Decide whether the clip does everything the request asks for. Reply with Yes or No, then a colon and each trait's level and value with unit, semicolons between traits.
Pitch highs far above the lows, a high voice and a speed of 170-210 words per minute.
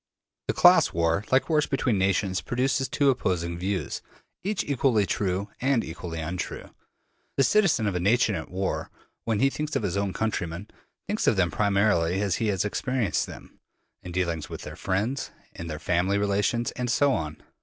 No: wide, 5.8 semitones; low, 100 Hz; average, 175 wpm